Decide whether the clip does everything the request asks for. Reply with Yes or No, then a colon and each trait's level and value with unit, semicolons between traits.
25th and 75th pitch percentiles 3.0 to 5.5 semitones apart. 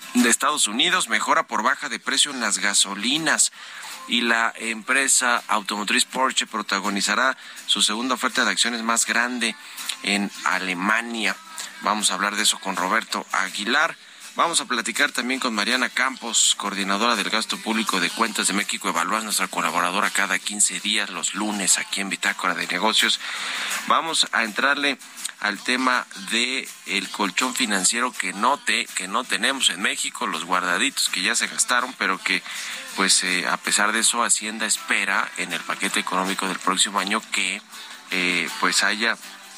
Yes: average, 3.3 semitones